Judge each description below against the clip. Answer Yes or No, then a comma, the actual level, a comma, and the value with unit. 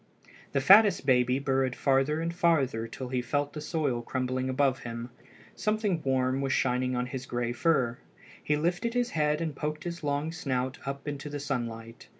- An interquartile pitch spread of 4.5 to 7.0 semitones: No, average, 3.2 semitones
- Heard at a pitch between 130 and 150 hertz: Yes, low, 135 Hz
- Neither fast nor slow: Yes, average, 175 wpm